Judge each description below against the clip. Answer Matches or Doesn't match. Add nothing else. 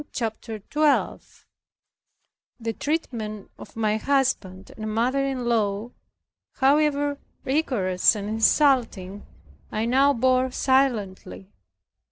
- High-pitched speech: Matches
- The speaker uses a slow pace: Matches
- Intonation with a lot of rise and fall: Doesn't match